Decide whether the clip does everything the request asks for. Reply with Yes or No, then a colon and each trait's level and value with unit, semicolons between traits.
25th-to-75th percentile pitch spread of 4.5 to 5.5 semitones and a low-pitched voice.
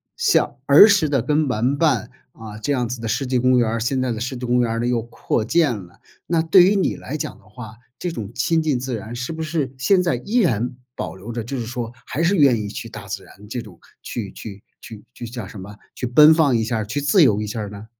Yes: average, 4.9 semitones; low, 125 Hz